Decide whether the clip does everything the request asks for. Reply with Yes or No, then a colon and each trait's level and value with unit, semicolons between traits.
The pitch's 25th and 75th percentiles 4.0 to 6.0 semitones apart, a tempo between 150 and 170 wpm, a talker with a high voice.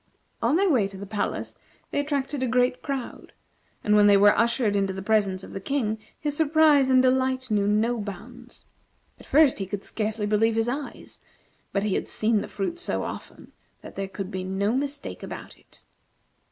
No: average, 4.6 semitones; average, 195 wpm; high, 225 Hz